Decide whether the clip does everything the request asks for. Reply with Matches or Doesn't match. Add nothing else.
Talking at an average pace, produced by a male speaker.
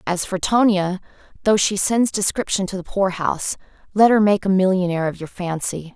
Doesn't match